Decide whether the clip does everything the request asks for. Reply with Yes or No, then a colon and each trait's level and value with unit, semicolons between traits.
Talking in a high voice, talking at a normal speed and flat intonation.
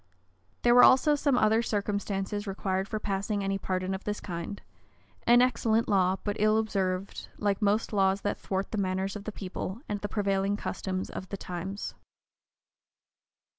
Yes: high, 200 Hz; average, 170 wpm; narrow, 2.0 semitones